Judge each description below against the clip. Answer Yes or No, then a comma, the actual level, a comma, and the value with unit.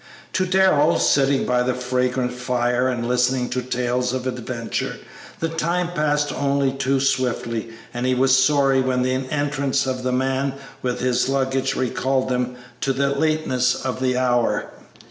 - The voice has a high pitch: No, low, 130 Hz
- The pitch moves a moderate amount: No, narrow, 1.7 semitones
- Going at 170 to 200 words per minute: No, average, 160 wpm